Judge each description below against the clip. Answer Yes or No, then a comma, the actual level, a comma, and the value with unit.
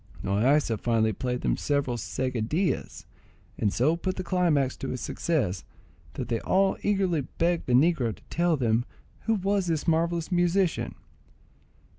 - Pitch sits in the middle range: Yes, medium, 155 Hz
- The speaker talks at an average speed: Yes, average, 145 wpm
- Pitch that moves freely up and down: Yes, wide, 6.2 semitones